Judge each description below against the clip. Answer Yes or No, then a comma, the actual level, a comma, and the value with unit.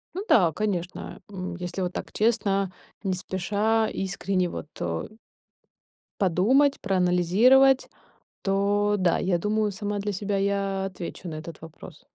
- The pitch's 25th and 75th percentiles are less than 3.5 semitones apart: Yes, narrow, 2.6 semitones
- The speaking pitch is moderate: No, high, 195 Hz